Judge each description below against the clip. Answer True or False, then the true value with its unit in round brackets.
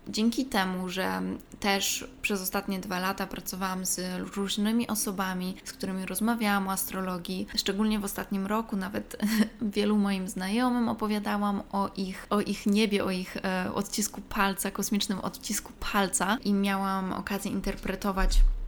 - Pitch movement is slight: True (1.8 semitones)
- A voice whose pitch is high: True (200 Hz)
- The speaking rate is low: False (135 wpm)